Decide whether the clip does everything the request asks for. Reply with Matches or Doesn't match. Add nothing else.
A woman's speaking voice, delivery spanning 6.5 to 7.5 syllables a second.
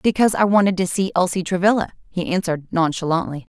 Matches